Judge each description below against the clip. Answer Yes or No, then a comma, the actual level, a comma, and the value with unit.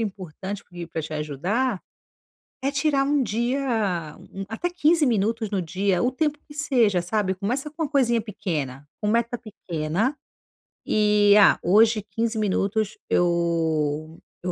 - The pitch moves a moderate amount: No, wide, 5.8 semitones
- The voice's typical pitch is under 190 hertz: No, high, 210 Hz